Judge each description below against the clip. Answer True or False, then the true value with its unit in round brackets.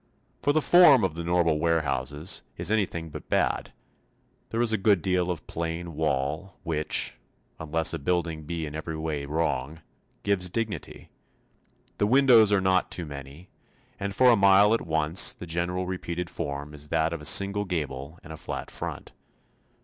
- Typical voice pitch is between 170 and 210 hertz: False (85 Hz)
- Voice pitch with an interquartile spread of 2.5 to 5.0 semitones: True (4.0 semitones)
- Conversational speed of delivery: True (170 wpm)